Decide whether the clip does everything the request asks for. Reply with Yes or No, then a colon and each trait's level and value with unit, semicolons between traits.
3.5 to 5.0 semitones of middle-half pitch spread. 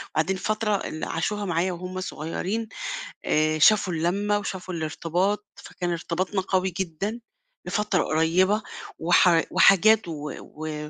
Yes: average, 3.8 semitones